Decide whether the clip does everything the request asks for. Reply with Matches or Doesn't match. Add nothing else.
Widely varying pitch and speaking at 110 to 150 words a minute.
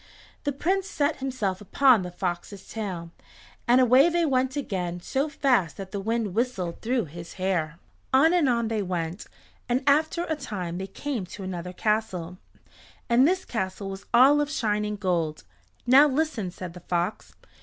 Doesn't match